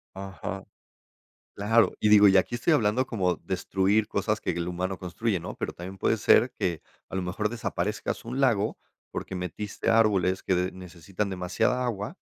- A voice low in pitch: Yes, low, 100 Hz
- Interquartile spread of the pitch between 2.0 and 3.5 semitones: Yes, average, 2.9 semitones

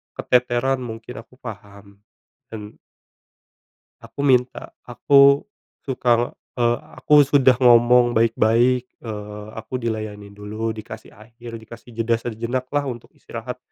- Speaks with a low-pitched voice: Yes, low, 120 Hz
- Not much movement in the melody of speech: Yes, narrow, 2.2 semitones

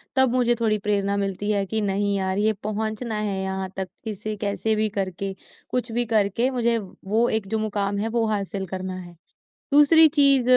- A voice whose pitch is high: Yes, high, 210 Hz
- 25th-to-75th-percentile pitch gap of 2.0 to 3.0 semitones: Yes, narrow, 2.6 semitones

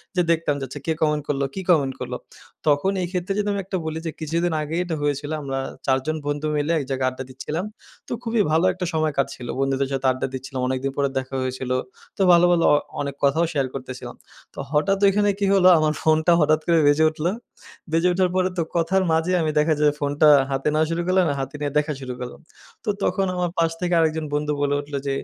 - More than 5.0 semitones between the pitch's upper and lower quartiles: No, average, 3.7 semitones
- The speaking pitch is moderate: Yes, medium, 155 Hz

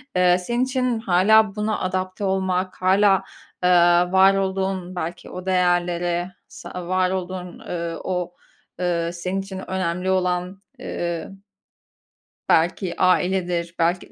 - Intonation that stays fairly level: Yes, narrow, 1.3 semitones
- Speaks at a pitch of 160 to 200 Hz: Yes, medium, 185 Hz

